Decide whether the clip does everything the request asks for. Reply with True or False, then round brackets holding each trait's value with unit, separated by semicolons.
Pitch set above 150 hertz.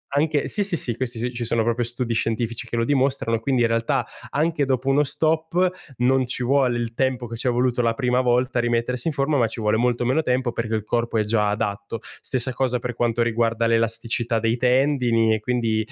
False (120 Hz)